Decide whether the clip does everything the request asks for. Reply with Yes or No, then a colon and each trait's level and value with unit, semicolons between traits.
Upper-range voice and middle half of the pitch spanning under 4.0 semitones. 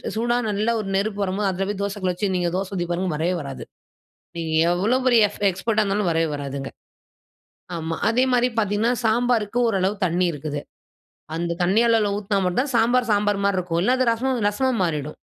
No: high, 200 Hz; average, 4.3 semitones